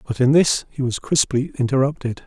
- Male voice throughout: Yes, male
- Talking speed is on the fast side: No, average, 185 wpm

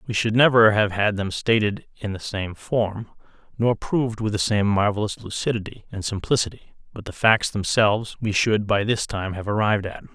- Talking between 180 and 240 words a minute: Yes, average, 190 wpm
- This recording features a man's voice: Yes, male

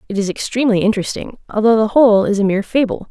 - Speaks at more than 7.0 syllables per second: Yes, 7.5 syllables/s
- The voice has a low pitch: No, high, 215 Hz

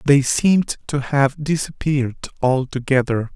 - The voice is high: No, medium, 140 Hz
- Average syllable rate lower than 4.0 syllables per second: No, 4.5 syllables/s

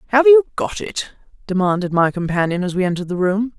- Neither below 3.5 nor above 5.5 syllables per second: No, 6.1 syllables/s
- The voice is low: No, high, 195 Hz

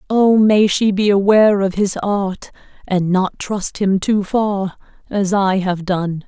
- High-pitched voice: Yes, high, 195 Hz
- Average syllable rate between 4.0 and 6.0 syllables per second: No, 3.5 syllables/s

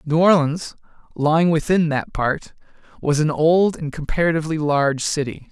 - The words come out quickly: No, average, 140 wpm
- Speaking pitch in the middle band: Yes, medium, 155 Hz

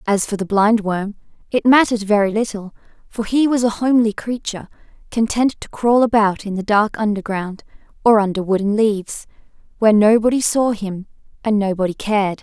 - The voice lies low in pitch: No, high, 215 Hz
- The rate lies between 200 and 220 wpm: No, average, 165 wpm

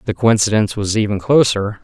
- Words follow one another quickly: No, average, 165 wpm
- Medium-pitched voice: No, low, 105 Hz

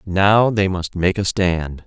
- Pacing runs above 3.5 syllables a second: No, 3.4 syllables/s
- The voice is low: Yes, very low, 95 Hz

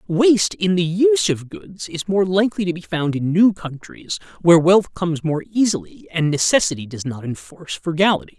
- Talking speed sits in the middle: Yes, average, 185 wpm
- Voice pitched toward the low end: No, medium, 175 Hz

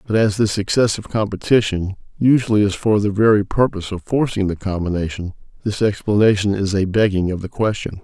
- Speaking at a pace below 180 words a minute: Yes, average, 170 wpm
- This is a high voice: No, low, 105 Hz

